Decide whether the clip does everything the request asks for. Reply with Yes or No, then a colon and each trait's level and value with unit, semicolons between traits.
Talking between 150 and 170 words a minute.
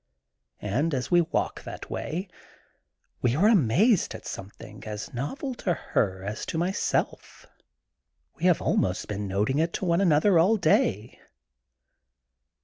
No: average, 140 wpm